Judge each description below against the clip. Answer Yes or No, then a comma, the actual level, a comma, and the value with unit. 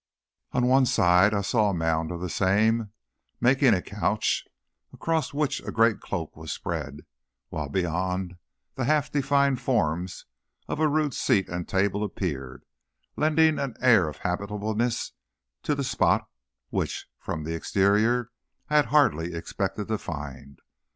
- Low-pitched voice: Yes, low, 100 Hz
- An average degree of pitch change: No, wide, 6.4 semitones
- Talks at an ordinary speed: Yes, average, 145 wpm